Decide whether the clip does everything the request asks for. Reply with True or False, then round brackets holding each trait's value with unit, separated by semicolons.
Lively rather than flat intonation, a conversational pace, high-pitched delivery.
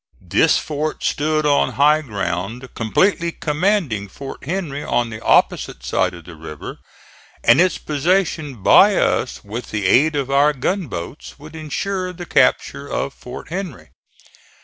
False (5.8 semitones; 145 wpm; 145 Hz)